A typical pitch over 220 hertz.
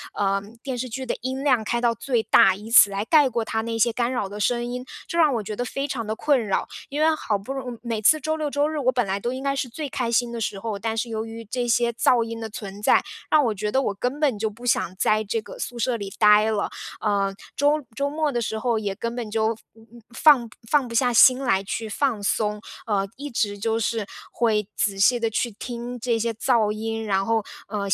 Yes: high, 230 Hz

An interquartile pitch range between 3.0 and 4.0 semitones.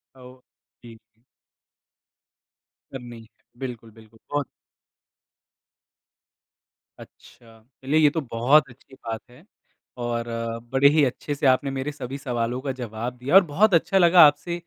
Yes: average, 3.7 semitones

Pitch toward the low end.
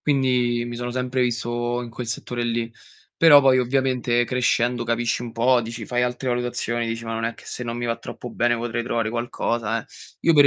Yes: low, 120 Hz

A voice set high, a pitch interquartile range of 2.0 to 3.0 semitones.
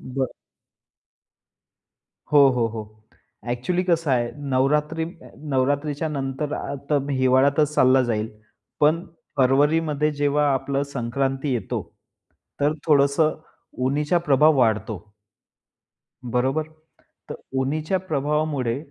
No: medium, 140 Hz; average, 2.7 semitones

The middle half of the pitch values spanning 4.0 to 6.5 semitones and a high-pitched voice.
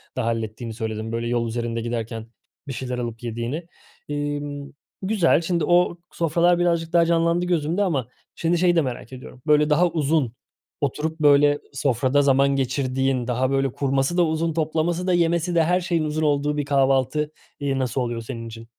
No: average, 4.8 semitones; medium, 145 Hz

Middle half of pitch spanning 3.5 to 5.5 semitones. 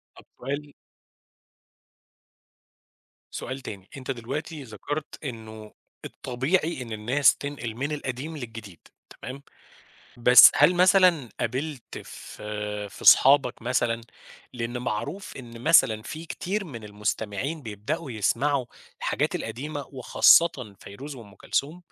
Yes: average, 4.7 semitones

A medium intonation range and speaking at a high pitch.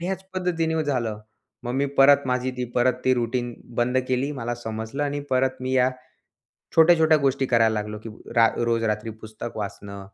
No: average, 3.7 semitones; low, 125 Hz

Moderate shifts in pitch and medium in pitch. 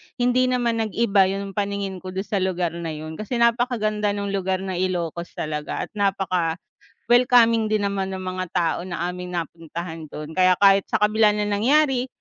No: average, 3.6 semitones; high, 195 Hz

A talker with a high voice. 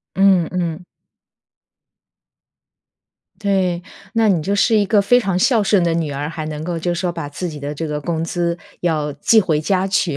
No: medium, 175 Hz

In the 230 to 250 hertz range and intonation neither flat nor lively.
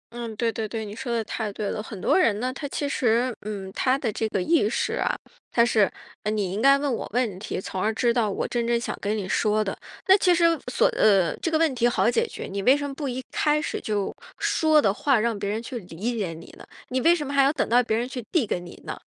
Yes: high, 235 Hz; average, 4.4 semitones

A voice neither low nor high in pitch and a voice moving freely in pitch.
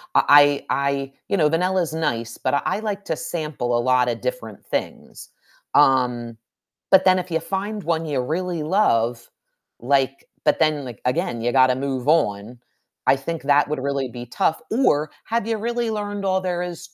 Yes: medium, 150 Hz; wide, 6.3 semitones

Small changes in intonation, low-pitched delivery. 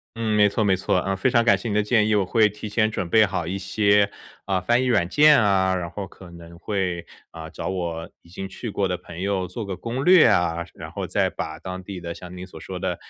No: average, 3.1 semitones; very low, 95 Hz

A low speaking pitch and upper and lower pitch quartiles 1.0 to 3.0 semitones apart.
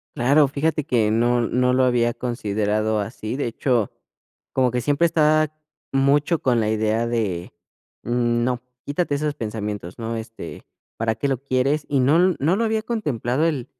No: low, 125 Hz; average, 4.3 semitones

